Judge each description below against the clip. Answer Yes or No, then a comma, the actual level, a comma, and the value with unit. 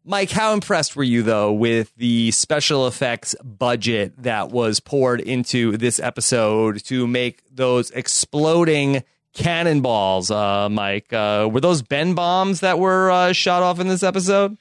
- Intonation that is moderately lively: No, wide, 7.3 semitones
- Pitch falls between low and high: No, low, 130 Hz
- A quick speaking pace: No, average, 150 wpm